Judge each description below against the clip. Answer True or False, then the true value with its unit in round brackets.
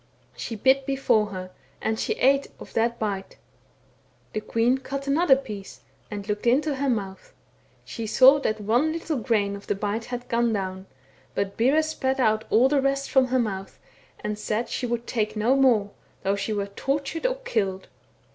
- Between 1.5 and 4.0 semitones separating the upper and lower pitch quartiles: False (4.5 semitones)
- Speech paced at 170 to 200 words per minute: True (180 wpm)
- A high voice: True (235 Hz)